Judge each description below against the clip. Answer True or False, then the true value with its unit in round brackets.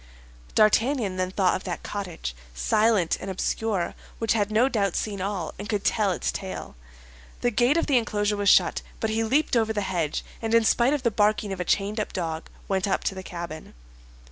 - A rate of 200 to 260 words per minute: True (205 wpm)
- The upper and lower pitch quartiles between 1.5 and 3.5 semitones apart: True (3.1 semitones)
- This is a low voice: False (205 Hz)